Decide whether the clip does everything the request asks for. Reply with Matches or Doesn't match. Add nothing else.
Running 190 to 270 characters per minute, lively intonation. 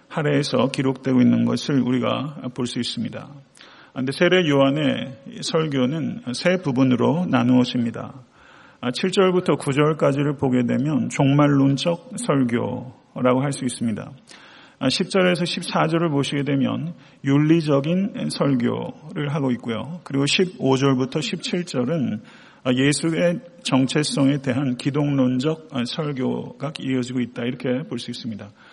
Doesn't match